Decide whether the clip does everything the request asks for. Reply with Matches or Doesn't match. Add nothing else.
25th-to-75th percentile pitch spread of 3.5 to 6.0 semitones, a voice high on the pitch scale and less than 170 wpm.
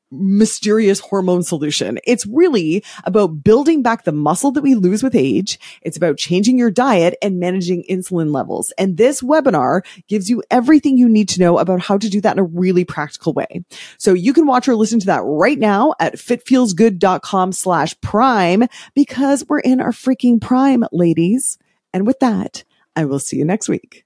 Doesn't match